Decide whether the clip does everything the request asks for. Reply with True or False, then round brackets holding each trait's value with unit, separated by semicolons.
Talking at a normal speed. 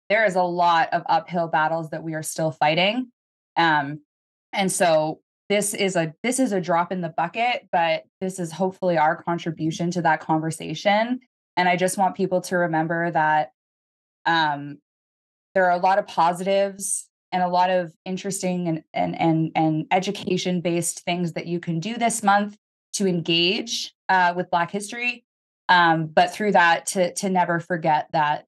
True (175 wpm)